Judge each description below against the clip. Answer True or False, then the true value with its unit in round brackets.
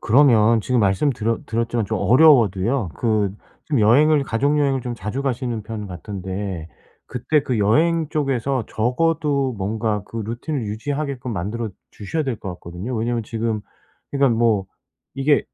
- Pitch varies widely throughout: False (4.5 semitones)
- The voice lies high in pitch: False (115 Hz)